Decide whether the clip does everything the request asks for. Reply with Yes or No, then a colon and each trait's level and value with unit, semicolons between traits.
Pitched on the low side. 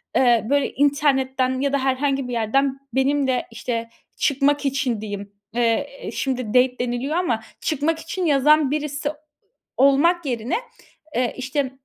No: very high, 270 Hz